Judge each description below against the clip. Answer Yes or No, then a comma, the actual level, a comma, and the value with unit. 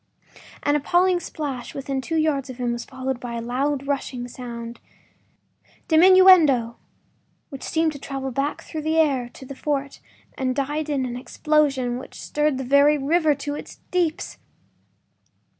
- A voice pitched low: No, very high, 280 Hz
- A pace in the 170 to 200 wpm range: No, average, 160 wpm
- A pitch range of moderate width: Yes, average, 3.1 semitones